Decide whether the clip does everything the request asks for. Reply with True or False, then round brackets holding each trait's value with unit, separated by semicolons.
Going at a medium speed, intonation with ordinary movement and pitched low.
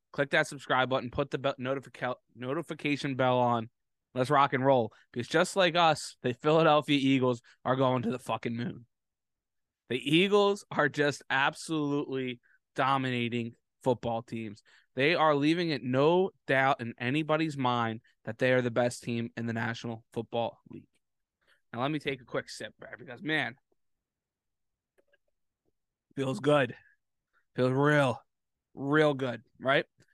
True (145 wpm; 3.6 semitones; 130 Hz)